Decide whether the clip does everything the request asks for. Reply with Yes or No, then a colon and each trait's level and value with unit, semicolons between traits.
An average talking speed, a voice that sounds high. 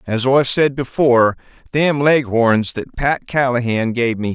No: average, 150 wpm; low, 125 Hz